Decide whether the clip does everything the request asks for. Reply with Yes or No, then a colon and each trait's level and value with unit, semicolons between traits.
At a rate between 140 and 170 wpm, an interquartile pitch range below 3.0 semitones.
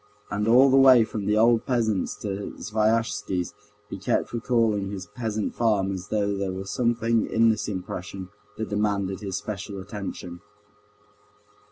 Yes: average, 150 wpm; narrow, 2.6 semitones